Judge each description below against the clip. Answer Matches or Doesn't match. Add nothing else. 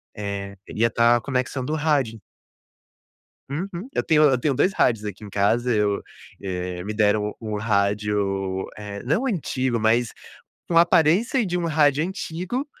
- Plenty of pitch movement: Matches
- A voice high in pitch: Doesn't match